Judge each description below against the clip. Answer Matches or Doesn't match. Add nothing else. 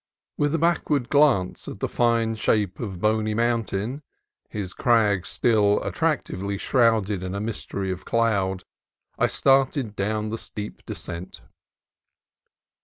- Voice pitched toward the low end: Matches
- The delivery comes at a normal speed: Doesn't match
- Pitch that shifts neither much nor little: Matches